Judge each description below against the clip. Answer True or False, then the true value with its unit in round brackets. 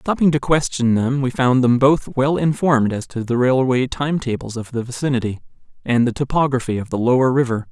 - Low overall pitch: True (130 Hz)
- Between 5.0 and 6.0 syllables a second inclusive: True (5.5 syllables/s)